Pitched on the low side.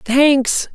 No: very high, 270 Hz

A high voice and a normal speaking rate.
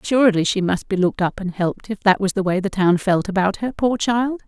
No: high, 200 Hz; fast, 270 wpm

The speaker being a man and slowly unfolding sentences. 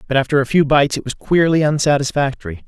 No: male; average, 200 wpm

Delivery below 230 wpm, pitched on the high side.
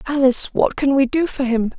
No: fast, 235 wpm; very high, 265 Hz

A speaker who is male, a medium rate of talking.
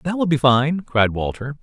No: male; fast, 220 wpm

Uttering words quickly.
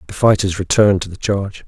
Yes: fast, 215 wpm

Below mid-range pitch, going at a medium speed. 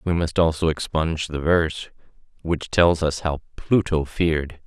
Yes: very low, 80 Hz; average, 155 wpm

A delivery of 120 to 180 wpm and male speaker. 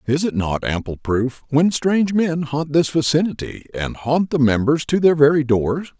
No: average, 190 wpm; male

